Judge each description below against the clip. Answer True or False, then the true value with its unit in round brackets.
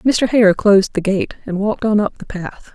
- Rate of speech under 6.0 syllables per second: True (5.0 syllables/s)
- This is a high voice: True (200 Hz)